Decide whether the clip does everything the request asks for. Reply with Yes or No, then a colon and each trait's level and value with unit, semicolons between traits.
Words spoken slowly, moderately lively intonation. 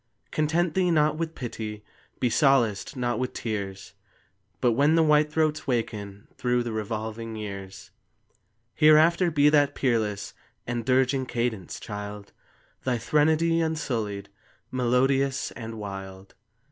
No: slow, 120 wpm; wide, 5.9 semitones